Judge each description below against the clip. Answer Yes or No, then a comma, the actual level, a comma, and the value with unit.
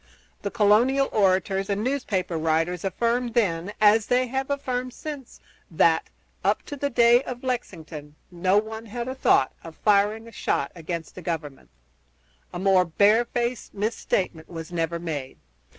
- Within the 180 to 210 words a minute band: No, average, 150 wpm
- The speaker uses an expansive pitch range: Yes, wide, 6.0 semitones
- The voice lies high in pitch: Yes, high, 205 Hz